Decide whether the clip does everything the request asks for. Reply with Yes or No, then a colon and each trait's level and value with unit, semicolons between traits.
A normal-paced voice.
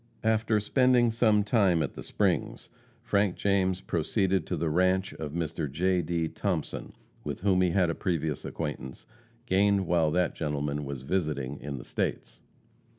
Yes: average, 155 wpm